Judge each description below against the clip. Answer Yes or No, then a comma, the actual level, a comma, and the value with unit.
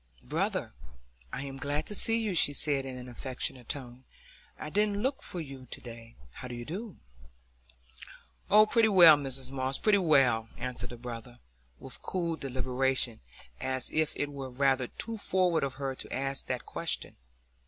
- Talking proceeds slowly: No, average, 165 wpm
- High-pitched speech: No, low, 135 Hz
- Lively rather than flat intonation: No, average, 5.0 semitones